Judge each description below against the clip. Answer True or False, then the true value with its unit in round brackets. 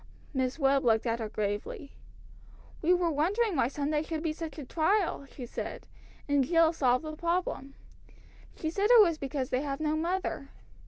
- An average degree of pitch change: True (3.9 semitones)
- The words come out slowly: False (175 wpm)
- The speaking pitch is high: True (300 Hz)